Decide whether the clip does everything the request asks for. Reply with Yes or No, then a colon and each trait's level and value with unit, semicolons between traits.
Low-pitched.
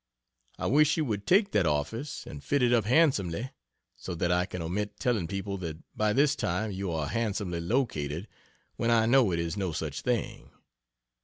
Yes: low, 100 Hz